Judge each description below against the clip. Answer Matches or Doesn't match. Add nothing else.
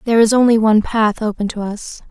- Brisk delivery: Matches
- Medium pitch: Doesn't match